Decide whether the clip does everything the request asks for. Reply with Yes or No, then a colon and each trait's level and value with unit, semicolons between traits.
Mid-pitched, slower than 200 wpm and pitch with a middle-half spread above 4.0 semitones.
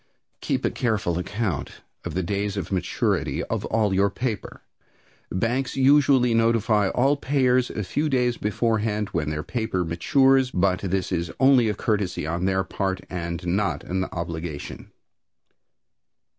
No: low, 100 Hz; average, 140 wpm; average, 5.1 semitones